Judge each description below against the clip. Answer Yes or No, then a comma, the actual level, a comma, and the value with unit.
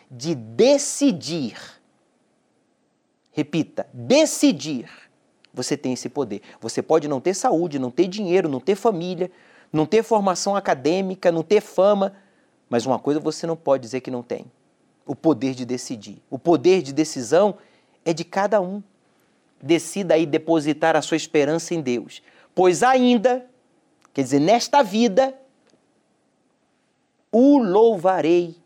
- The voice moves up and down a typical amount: No, wide, 5.9 semitones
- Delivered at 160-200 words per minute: No, average, 135 wpm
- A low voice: No, medium, 170 Hz